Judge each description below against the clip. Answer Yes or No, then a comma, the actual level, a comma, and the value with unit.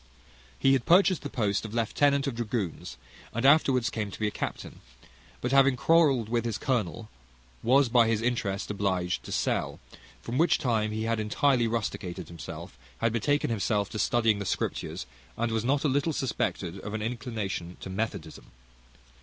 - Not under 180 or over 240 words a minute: No, average, 170 wpm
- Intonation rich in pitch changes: No, average, 3.9 semitones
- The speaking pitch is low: Yes, low, 115 Hz